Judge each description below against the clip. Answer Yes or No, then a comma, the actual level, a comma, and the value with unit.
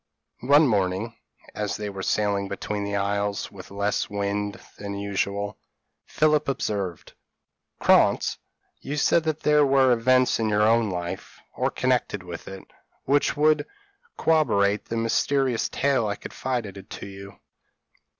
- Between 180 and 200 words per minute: No, slow, 135 wpm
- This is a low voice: Yes, low, 105 Hz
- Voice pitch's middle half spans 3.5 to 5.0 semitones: Yes, average, 4.6 semitones